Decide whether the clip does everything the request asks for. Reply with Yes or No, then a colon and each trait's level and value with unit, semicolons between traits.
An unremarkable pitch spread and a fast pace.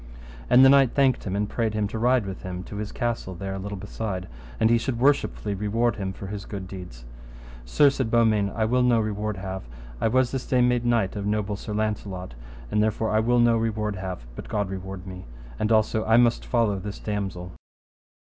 Yes: average, 3.3 semitones; fast, 210 wpm